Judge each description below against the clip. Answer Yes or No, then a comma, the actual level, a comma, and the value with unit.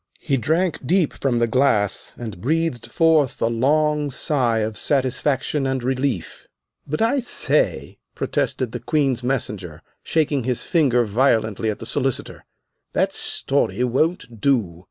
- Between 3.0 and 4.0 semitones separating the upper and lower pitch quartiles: No, average, 4.5 semitones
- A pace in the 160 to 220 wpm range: No, slow, 135 wpm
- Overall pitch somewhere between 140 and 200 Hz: No, low, 130 Hz